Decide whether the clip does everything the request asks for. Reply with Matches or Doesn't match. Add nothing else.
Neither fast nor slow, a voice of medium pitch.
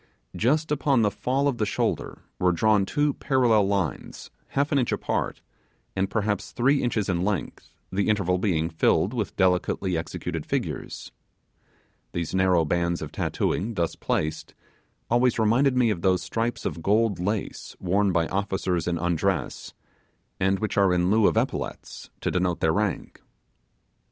Doesn't match